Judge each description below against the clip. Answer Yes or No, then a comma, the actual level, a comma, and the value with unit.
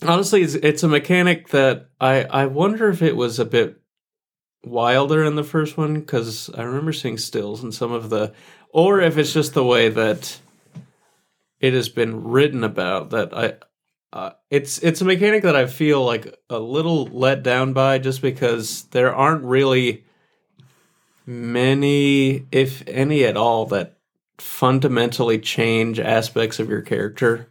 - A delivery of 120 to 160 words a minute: Yes, average, 155 wpm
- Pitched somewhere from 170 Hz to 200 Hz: No, low, 135 Hz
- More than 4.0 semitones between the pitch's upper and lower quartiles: Yes, average, 4.4 semitones